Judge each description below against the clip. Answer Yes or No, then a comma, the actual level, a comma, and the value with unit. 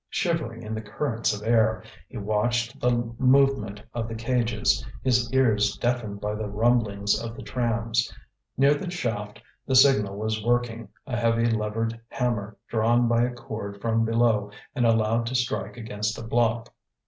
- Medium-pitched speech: No, low, 115 Hz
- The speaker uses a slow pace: No, average, 160 wpm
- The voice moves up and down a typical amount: No, narrow, 2.0 semitones